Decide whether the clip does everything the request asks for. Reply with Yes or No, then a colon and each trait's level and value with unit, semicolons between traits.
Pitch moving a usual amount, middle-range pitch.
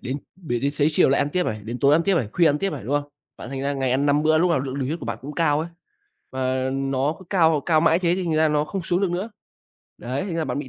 Yes: average, 3.8 semitones; medium, 145 Hz